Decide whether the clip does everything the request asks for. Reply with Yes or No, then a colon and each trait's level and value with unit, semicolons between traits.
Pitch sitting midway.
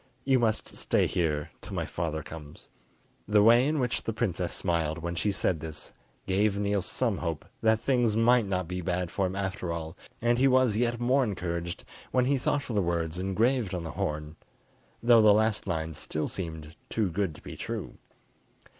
No: very low, 95 Hz